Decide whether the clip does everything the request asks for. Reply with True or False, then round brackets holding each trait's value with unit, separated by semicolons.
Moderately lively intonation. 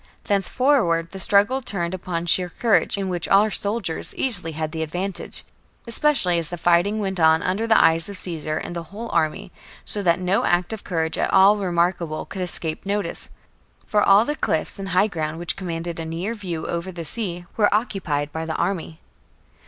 True (3.4 semitones)